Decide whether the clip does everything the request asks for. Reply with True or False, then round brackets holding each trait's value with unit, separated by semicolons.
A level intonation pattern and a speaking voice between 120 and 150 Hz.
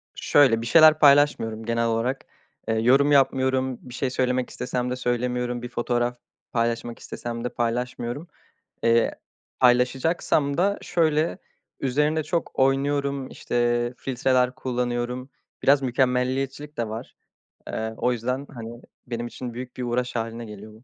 True (2.3 semitones; 125 Hz)